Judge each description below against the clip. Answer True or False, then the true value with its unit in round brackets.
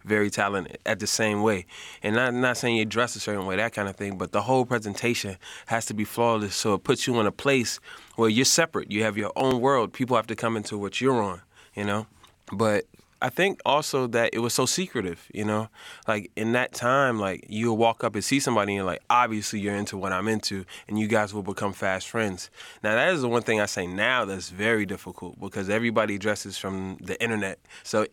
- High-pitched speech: False (105 Hz)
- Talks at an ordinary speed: False (235 wpm)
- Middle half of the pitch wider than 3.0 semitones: False (2.7 semitones)